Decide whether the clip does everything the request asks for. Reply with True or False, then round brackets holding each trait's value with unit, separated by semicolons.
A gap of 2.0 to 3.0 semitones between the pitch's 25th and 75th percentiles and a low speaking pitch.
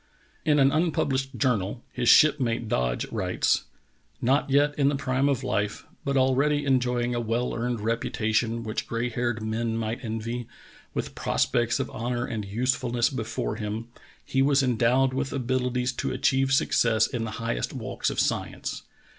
True (2.7 semitones; 120 Hz)